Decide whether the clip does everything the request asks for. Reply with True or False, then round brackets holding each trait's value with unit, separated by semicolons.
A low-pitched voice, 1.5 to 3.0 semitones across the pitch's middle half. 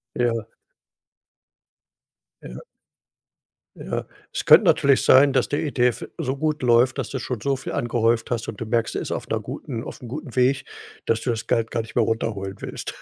True (120 Hz; 2.6 semitones)